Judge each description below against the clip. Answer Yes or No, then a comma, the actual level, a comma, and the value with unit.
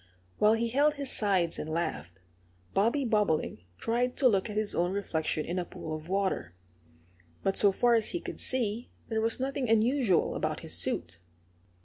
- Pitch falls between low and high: No, high, 210 Hz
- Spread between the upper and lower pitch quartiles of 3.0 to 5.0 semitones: No, wide, 5.5 semitones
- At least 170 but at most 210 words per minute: Yes, average, 175 wpm